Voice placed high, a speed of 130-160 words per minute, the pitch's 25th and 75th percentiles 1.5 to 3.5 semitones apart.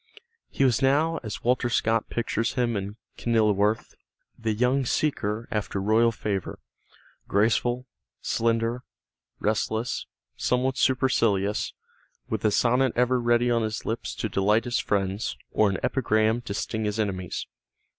No: low, 115 Hz; slow, 135 wpm; narrow, 2.6 semitones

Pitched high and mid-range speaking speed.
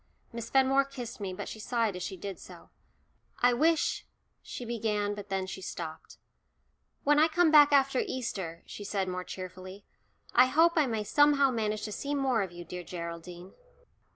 Yes: high, 220 Hz; average, 180 wpm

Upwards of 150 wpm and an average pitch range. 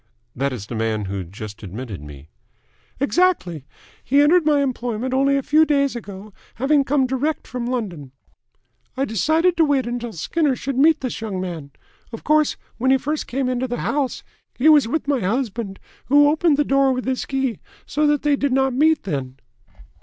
No: average, 185 wpm; wide, 7.0 semitones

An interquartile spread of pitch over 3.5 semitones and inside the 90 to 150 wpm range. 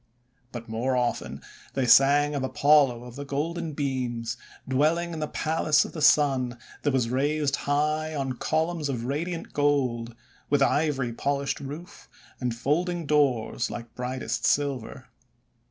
No: average, 3.2 semitones; average, 140 wpm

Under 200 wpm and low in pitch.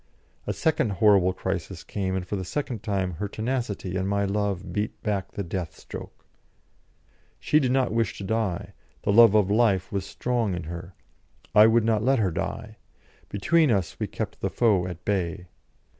Yes: average, 180 wpm; low, 100 Hz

